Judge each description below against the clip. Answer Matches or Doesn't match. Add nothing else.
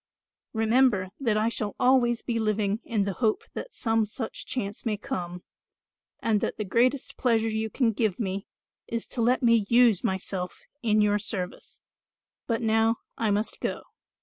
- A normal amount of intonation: Doesn't match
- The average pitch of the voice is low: Doesn't match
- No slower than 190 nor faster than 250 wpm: Doesn't match